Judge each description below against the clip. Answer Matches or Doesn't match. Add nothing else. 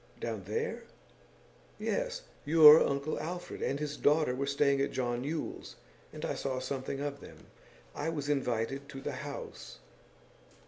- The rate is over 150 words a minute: Doesn't match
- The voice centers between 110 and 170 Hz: Matches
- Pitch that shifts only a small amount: Matches